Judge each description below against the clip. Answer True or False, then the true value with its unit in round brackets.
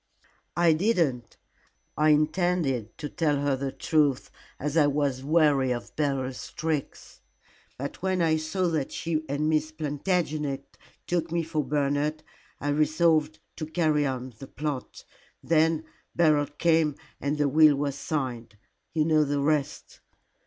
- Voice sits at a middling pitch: True (150 Hz)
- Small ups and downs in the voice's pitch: True (2.2 semitones)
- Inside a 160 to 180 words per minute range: False (140 wpm)